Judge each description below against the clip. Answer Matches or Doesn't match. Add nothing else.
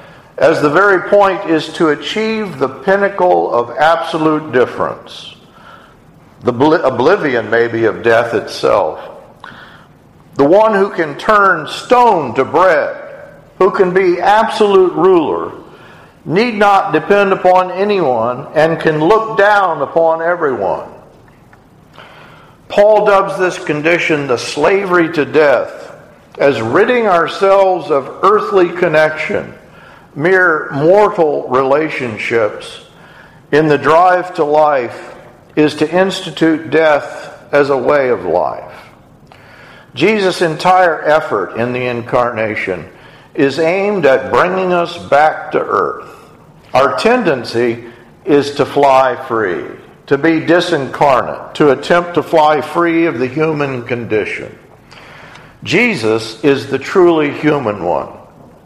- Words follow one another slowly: Matches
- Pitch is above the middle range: Doesn't match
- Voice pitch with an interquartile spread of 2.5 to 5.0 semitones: Doesn't match